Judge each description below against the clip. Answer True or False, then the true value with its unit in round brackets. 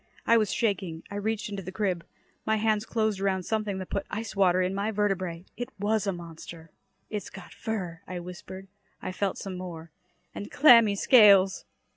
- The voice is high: True (195 Hz)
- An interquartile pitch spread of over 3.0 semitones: False (2.7 semitones)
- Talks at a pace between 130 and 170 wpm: False (180 wpm)